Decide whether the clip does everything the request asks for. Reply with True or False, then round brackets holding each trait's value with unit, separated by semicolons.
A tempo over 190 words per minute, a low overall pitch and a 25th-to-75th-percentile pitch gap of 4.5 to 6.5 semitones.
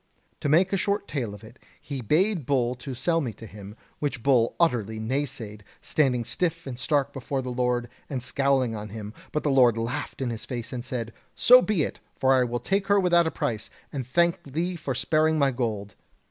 True (205 wpm; 130 Hz; 4.8 semitones)